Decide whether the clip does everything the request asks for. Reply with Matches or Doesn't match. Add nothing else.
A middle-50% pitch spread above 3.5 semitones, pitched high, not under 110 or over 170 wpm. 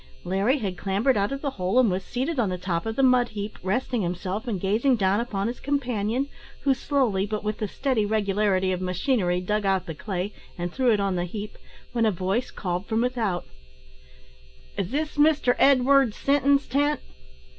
Doesn't match